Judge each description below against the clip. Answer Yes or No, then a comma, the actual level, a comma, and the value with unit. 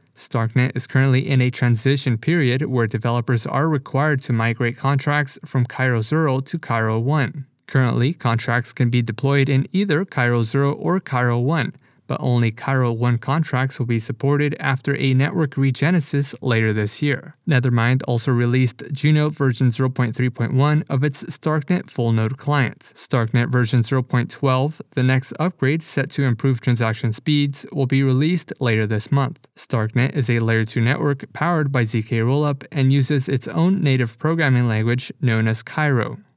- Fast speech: No, average, 160 wpm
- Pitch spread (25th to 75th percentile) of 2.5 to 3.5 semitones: Yes, average, 3.0 semitones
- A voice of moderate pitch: No, low, 130 Hz